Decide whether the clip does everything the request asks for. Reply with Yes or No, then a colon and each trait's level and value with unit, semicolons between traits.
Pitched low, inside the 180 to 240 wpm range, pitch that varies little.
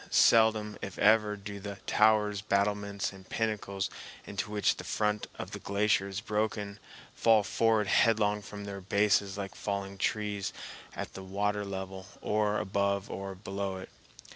No: low, 100 Hz; average, 150 wpm; narrow, 1.2 semitones